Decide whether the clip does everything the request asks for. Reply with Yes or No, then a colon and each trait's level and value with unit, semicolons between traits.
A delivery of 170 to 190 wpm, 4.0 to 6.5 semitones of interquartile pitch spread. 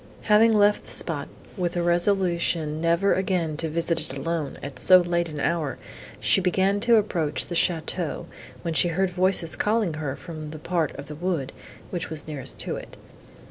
No: average, 180 wpm; average, 3.1 semitones